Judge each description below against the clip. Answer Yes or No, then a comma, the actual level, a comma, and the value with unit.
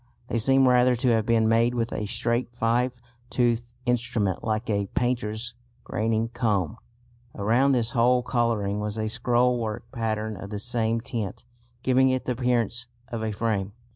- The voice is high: No, low, 115 Hz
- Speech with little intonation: Yes, narrow, 2.1 semitones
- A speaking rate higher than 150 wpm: Yes, average, 160 wpm